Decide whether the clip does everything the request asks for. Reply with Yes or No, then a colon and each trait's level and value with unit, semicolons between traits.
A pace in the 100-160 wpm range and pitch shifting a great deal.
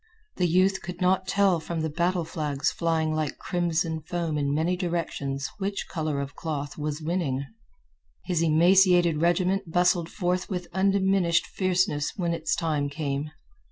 No: average, 150 wpm; average, 2.8 semitones